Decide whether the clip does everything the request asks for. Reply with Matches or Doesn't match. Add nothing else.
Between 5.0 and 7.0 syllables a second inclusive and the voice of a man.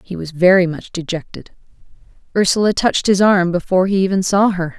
Doesn't match